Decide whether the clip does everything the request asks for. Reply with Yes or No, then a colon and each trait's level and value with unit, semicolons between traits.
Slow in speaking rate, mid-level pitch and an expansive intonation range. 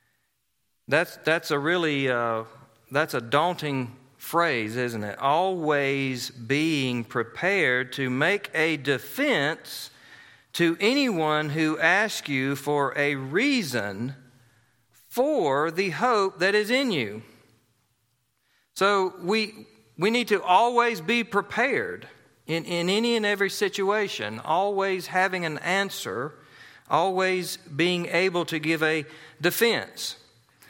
Yes: slow, 115 wpm; medium, 160 Hz; wide, 7.0 semitones